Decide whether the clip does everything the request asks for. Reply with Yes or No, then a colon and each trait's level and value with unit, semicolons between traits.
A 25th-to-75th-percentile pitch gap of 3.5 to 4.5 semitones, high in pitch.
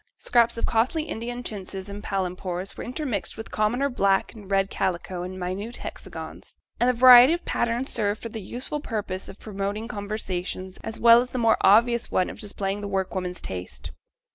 Yes: average, 3.8 semitones; high, 210 Hz